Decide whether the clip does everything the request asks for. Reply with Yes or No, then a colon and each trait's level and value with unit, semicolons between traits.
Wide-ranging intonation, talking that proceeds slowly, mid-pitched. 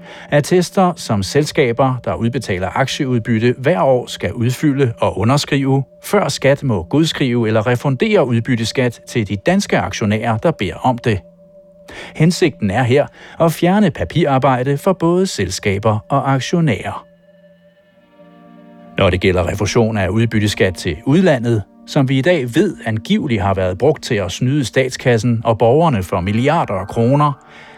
No: wide, 5.9 semitones; slow, 140 wpm; low, 130 Hz